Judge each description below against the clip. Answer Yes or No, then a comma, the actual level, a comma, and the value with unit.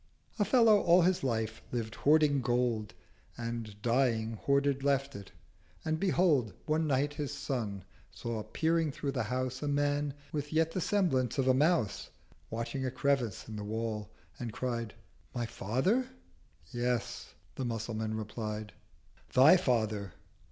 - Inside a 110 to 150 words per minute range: Yes, average, 140 wpm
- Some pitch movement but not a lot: Yes, average, 4.7 semitones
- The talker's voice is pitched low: Yes, low, 130 Hz